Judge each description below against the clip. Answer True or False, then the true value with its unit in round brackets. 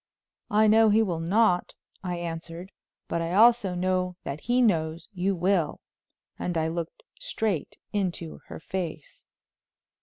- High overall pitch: False (180 Hz)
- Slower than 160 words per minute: True (140 wpm)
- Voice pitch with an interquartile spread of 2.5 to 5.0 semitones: True (3.8 semitones)